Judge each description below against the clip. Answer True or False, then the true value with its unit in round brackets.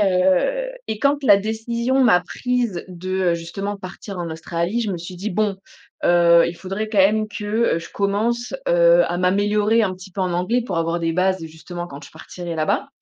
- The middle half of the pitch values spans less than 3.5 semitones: False (4.1 semitones)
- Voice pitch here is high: True (195 Hz)